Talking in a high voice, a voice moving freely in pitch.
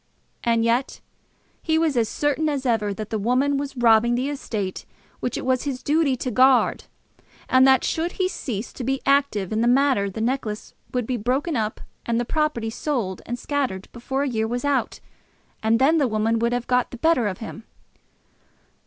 No: very high, 250 Hz; average, 3.7 semitones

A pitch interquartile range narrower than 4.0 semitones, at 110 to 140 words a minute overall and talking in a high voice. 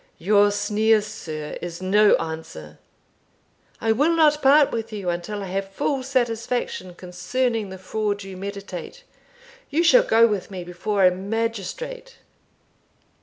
No: average, 4.4 semitones; slow, 135 wpm; high, 205 Hz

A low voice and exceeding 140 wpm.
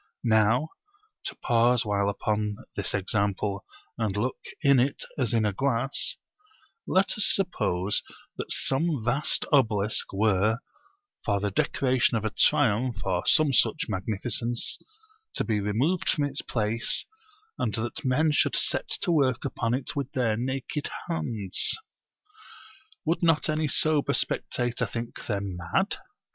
No: low, 115 Hz; slow, 135 wpm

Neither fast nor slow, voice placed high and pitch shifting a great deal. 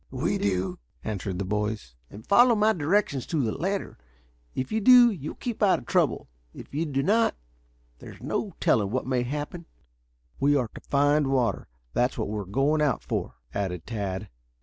No: average, 180 wpm; low, 135 Hz; wide, 8.4 semitones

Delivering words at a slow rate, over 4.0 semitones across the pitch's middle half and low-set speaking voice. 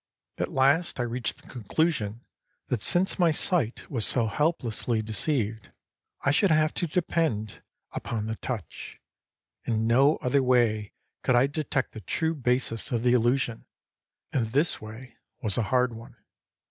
No: average, 150 wpm; average, 4.7 semitones; low, 125 Hz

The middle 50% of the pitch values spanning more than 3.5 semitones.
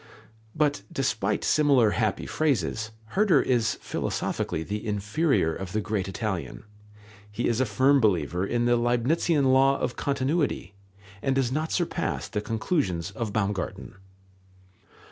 Yes: average, 5.3 semitones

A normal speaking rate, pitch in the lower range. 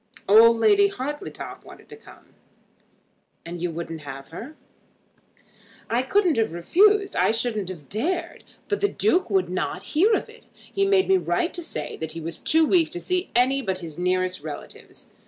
No: average, 175 wpm; high, 240 Hz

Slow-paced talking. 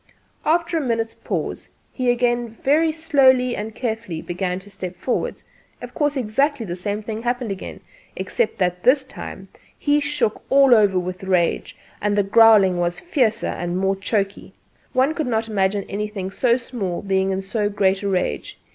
No: average, 170 wpm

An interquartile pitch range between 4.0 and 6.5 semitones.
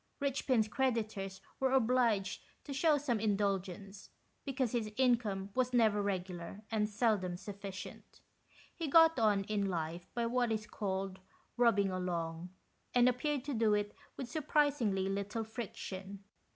Yes: average, 4.3 semitones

